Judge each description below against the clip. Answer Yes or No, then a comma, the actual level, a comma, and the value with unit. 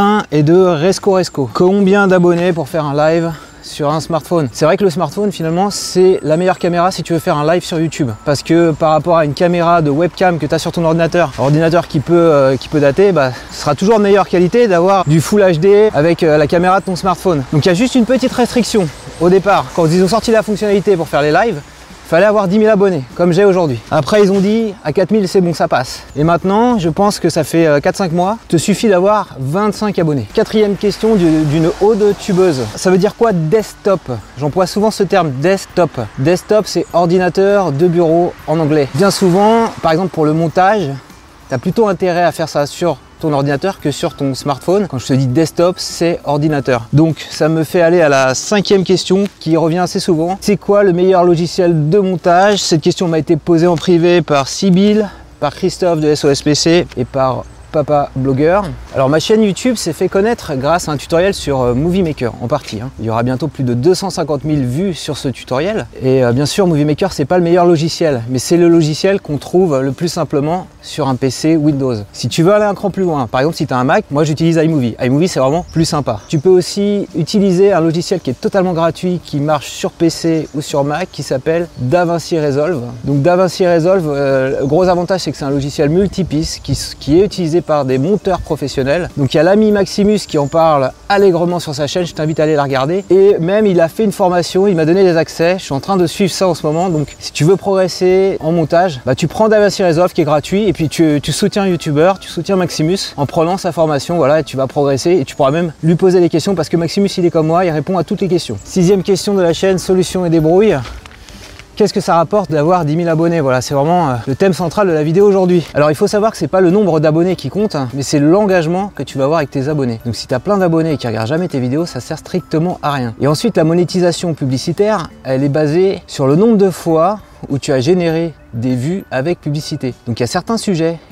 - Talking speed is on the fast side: Yes, fast, 235 wpm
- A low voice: No, medium, 170 Hz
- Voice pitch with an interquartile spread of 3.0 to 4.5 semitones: Yes, average, 4.2 semitones